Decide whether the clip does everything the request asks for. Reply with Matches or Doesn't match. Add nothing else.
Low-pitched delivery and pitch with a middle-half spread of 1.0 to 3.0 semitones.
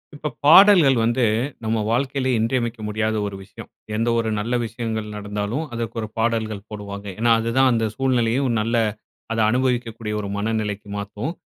Matches